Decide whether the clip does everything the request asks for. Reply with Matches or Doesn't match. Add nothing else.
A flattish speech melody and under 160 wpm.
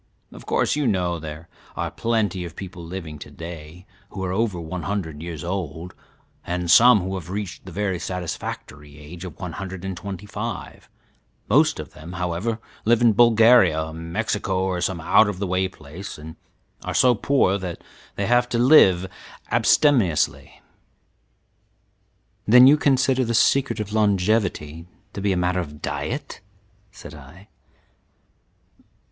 Doesn't match